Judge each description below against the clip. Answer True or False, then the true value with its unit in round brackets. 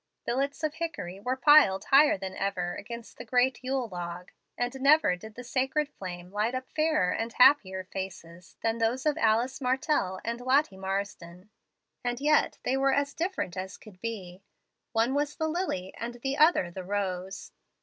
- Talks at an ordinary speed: True (170 wpm)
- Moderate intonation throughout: False (6.3 semitones)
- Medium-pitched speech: False (235 Hz)